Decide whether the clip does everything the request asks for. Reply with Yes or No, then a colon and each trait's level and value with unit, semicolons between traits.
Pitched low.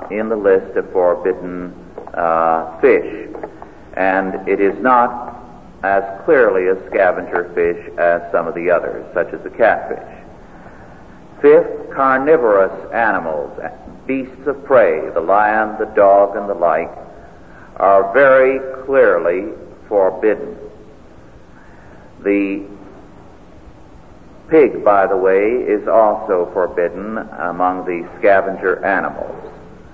Yes: low, 130 Hz